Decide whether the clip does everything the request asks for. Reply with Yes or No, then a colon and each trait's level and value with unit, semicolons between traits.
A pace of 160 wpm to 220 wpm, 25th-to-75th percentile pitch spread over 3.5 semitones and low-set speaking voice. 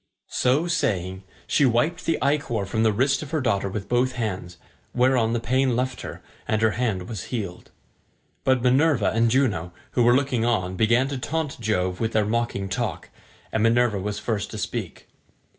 Yes: average, 180 wpm; average, 4.0 semitones; low, 115 Hz